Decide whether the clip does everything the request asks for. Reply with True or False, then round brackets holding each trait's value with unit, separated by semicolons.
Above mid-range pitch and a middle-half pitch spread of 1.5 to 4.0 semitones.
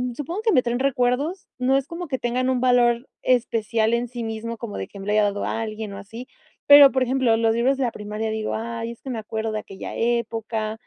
True (235 Hz; 2.6 semitones)